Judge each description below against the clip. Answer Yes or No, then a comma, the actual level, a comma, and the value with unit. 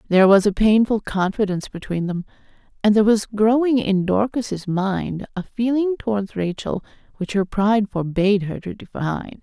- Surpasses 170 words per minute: No, average, 160 wpm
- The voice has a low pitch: No, high, 205 Hz